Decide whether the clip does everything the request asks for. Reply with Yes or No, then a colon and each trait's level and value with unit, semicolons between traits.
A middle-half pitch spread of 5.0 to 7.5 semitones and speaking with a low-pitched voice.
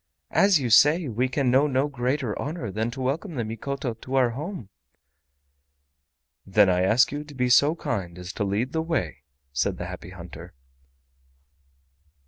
Yes: average, 5.3 semitones; low, 125 Hz